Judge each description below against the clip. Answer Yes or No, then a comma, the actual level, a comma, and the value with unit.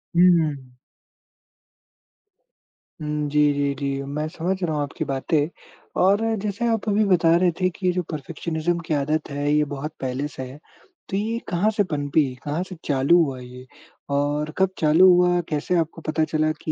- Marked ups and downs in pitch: No, average, 3.6 semitones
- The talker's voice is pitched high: No, medium, 155 Hz